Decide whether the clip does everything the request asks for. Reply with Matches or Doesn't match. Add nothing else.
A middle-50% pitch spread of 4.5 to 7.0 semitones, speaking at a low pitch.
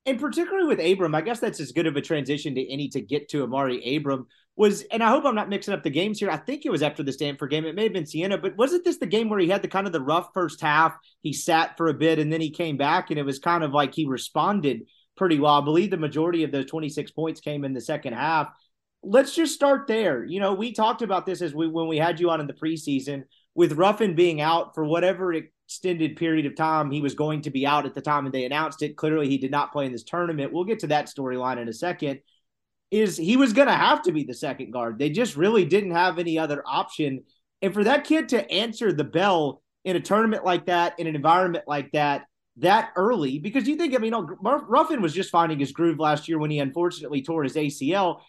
Doesn't match